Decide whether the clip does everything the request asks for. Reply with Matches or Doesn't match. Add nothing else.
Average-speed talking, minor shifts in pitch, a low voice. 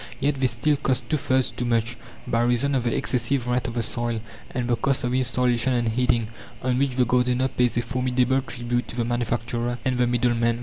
Doesn't match